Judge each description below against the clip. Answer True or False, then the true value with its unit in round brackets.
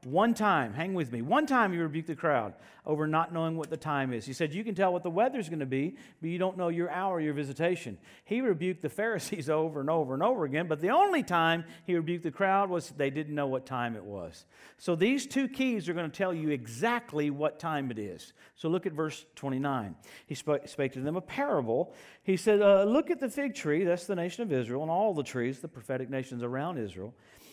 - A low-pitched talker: False (160 Hz)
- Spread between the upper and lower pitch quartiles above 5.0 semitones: True (5.4 semitones)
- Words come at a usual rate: False (240 wpm)